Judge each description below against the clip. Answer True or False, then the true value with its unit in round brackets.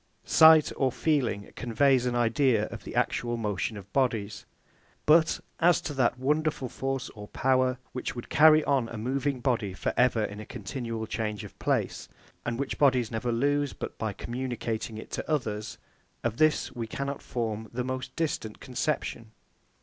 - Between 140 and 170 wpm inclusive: True (165 wpm)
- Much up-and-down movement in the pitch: False (3.6 semitones)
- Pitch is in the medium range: False (125 Hz)